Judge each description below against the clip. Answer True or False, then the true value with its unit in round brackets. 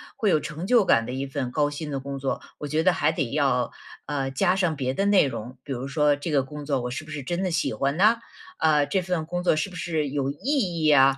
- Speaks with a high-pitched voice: False (150 Hz)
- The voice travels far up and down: False (3.3 semitones)